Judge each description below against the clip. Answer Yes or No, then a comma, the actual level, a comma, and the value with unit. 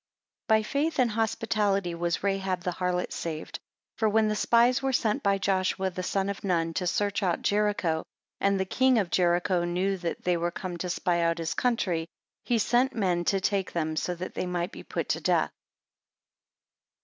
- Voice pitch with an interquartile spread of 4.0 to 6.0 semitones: No, average, 3.5 semitones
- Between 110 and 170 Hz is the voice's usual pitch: No, high, 190 Hz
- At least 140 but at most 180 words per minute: No, average, 195 wpm